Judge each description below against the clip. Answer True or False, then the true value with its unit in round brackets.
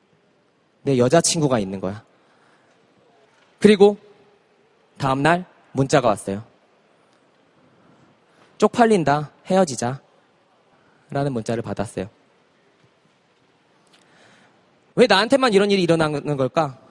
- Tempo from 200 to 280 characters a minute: False (190 characters per minute)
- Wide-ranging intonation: True (7.9 semitones)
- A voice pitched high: False (145 Hz)